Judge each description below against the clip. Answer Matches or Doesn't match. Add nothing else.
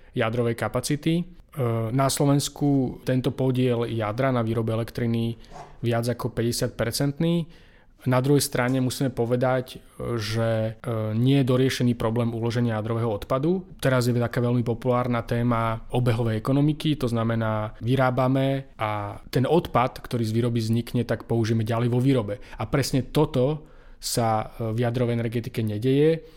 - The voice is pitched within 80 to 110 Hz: Doesn't match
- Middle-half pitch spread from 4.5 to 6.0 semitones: Doesn't match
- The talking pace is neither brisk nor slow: Matches